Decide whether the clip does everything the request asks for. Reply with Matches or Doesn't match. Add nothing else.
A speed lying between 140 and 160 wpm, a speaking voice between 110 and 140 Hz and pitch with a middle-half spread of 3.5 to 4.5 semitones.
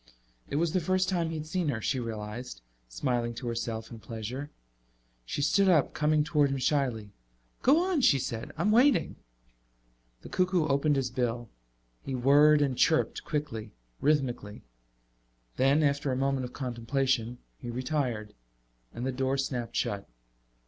Matches